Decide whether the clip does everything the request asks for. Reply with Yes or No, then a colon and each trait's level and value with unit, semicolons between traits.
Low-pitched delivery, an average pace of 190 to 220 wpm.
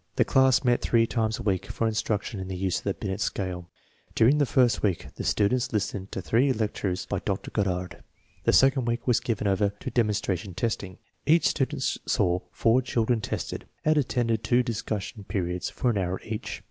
Yes: low, 110 Hz; average, 195 wpm